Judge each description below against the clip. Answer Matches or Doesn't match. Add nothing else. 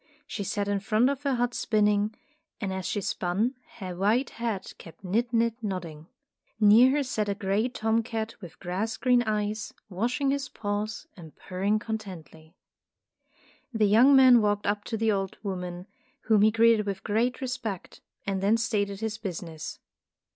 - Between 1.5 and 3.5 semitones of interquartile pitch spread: Matches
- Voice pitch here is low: Doesn't match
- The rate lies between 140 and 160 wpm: Doesn't match